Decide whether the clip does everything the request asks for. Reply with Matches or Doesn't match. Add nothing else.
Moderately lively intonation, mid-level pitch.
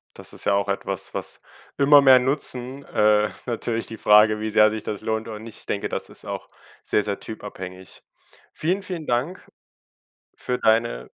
Doesn't match